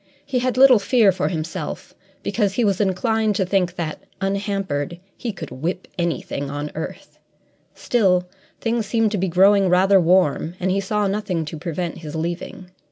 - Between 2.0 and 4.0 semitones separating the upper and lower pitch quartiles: Yes, average, 3.3 semitones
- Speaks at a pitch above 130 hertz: Yes, high, 190 Hz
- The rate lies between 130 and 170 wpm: Yes, average, 165 wpm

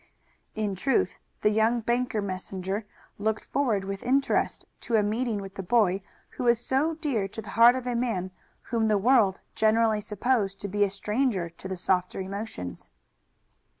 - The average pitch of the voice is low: No, high, 215 Hz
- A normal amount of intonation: Yes, average, 3.6 semitones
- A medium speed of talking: Yes, average, 170 wpm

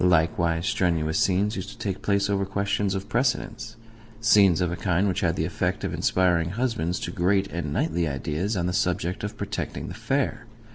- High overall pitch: No, very low, 95 Hz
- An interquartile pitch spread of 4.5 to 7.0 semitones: No, average, 3.0 semitones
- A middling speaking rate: Yes, average, 190 wpm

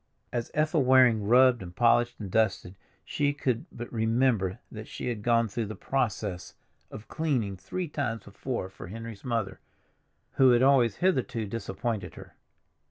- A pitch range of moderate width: Yes, average, 3.8 semitones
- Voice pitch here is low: Yes, low, 115 Hz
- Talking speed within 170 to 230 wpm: No, average, 155 wpm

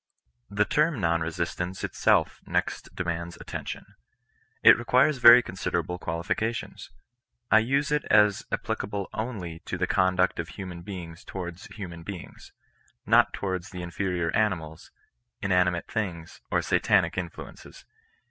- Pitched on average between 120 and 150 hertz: No, very low, 95 Hz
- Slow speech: Yes, slow, 130 wpm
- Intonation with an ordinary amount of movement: Yes, average, 3.7 semitones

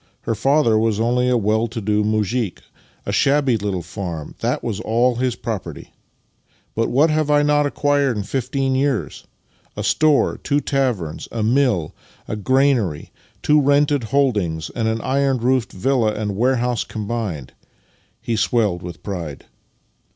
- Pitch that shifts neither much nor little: Yes, average, 4.4 semitones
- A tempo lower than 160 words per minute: Yes, average, 150 wpm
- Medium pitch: No, low, 115 Hz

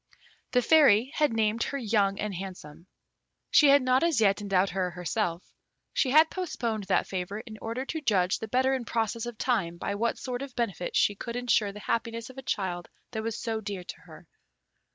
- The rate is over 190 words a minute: Yes, average, 200 wpm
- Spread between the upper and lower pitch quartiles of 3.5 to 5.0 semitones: Yes, average, 4.2 semitones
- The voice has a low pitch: No, high, 225 Hz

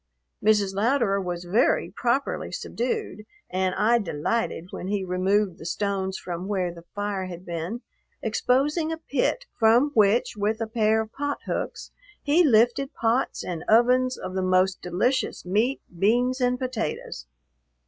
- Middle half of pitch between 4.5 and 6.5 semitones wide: Yes, average, 4.9 semitones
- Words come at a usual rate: Yes, average, 150 wpm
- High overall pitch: Yes, high, 215 Hz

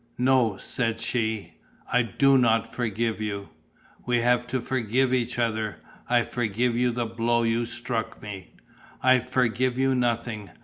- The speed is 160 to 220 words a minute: No, average, 145 wpm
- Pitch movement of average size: No, narrow, 1.8 semitones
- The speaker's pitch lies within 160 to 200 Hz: No, low, 120 Hz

